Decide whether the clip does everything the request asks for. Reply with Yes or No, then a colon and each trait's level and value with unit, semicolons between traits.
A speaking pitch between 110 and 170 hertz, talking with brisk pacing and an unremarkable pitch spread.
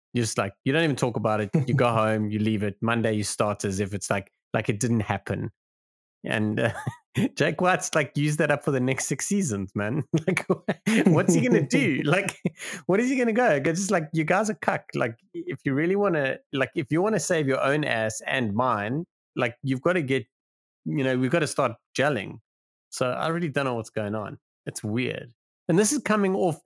No: low, 135 Hz; fast, 220 wpm; wide, 7.5 semitones